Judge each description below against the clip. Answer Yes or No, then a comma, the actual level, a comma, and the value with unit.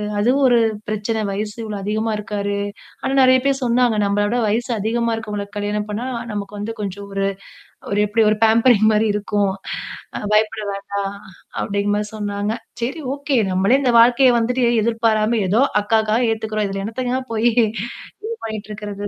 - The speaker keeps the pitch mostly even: Yes, narrow, 2.3 semitones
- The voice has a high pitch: Yes, high, 215 Hz